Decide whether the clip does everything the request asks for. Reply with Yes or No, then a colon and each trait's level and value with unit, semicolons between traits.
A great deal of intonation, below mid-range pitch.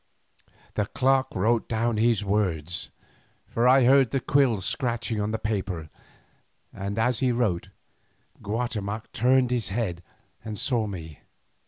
No: average, 3.5 semitones; low, 110 Hz